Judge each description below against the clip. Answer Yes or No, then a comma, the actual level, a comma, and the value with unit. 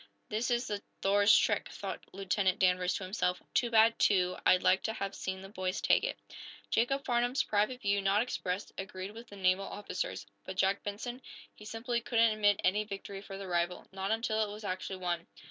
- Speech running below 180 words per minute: No, average, 195 wpm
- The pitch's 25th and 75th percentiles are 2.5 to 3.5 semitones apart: Yes, average, 2.9 semitones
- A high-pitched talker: Yes, high, 200 Hz